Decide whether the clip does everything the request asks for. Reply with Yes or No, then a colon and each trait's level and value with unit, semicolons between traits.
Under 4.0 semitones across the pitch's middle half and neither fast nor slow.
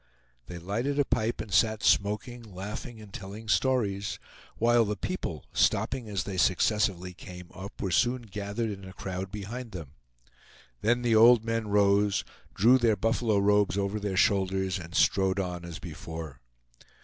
Yes: average, 3.2 semitones; average, 160 wpm